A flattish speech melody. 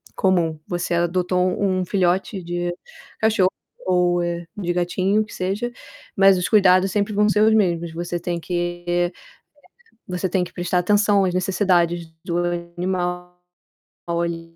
Yes: narrow, 1.7 semitones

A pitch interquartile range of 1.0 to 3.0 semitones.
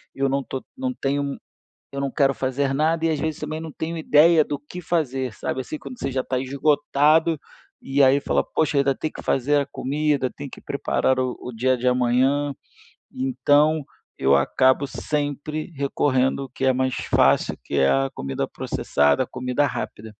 Yes: narrow, 2.5 semitones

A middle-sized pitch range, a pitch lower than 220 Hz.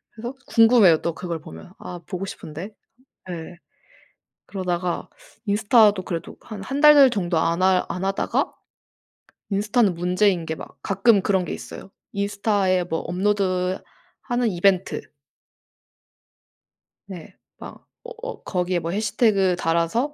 Yes: average, 3.0 semitones; high, 190 Hz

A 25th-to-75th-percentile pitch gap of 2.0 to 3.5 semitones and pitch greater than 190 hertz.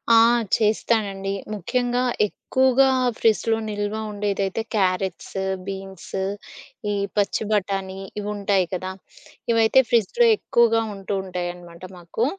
Yes: average, 2.8 semitones; high, 205 Hz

